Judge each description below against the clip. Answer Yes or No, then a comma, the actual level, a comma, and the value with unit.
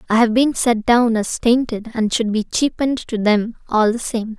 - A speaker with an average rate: No, fast, 220 wpm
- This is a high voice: Yes, high, 230 Hz